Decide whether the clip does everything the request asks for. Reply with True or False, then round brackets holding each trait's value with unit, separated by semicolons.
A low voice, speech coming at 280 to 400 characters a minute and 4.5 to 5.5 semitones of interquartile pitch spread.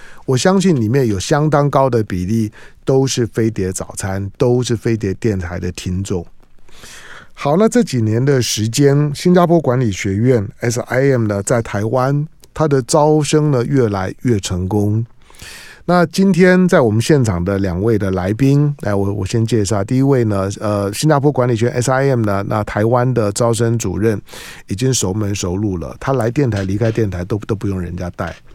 False (115 Hz; 265 characters per minute; 5.2 semitones)